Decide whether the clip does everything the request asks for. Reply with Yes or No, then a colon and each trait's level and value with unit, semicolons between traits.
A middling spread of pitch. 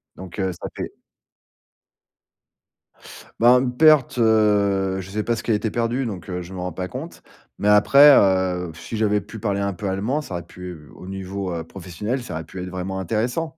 Yes: average, 4.0 semitones